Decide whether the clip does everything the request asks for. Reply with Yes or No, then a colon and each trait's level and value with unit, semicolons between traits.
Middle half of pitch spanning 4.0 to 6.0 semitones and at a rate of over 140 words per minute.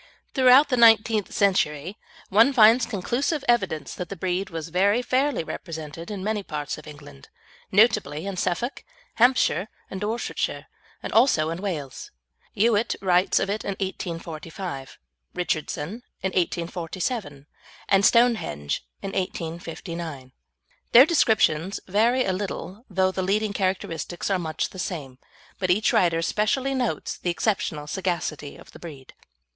No: average, 4.8 semitones; slow, 135 wpm